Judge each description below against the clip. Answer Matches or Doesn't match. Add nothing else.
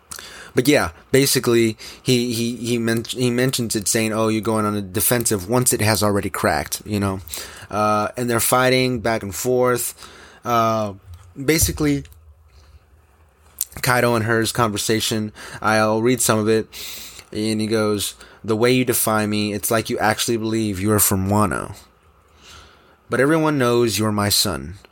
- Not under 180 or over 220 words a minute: Doesn't match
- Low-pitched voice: Matches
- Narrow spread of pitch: Doesn't match